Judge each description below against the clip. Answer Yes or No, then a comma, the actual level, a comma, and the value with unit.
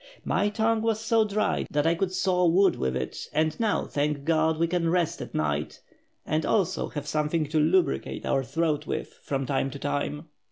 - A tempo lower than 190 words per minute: No, average, 195 wpm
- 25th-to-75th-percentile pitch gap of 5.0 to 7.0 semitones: No, average, 4.4 semitones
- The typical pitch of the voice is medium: Yes, medium, 160 Hz